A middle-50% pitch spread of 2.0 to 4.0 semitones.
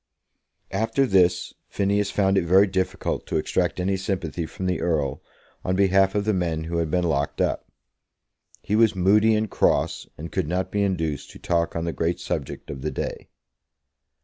Yes: average, 2.9 semitones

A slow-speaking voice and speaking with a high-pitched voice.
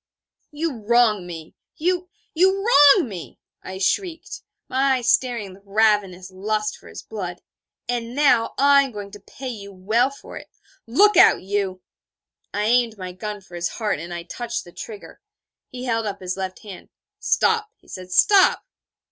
No: average, 170 wpm; high, 215 Hz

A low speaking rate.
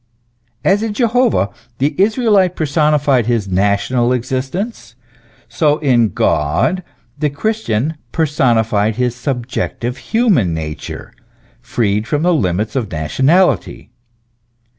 Yes: slow, 100 wpm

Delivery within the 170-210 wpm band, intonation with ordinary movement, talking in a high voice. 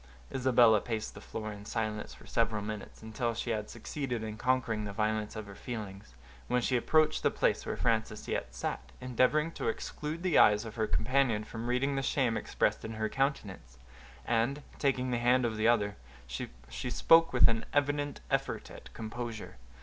No: average, 180 wpm; average, 3.2 semitones; low, 115 Hz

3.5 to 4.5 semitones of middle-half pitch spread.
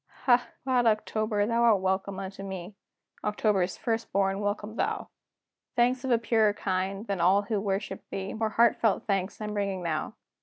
No: average, 2.7 semitones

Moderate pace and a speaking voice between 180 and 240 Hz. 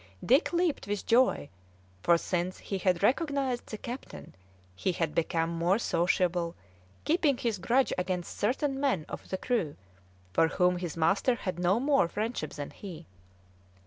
Yes: average, 150 wpm; high, 190 Hz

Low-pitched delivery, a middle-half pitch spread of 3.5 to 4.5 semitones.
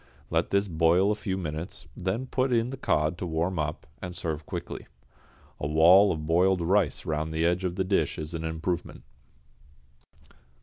No: very low, 85 Hz; average, 3.1 semitones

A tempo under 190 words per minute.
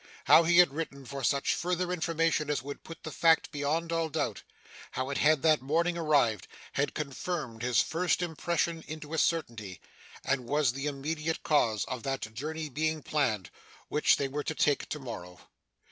Yes: average, 175 wpm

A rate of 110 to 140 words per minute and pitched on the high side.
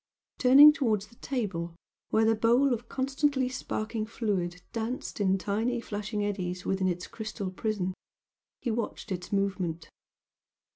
Yes: slow, 135 wpm; high, 215 Hz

